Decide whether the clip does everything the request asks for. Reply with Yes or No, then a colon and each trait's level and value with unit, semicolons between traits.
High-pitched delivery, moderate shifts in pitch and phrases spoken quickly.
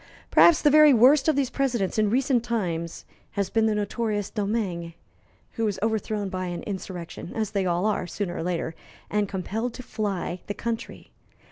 No: high, 210 Hz; average, 4.0 semitones; average, 175 wpm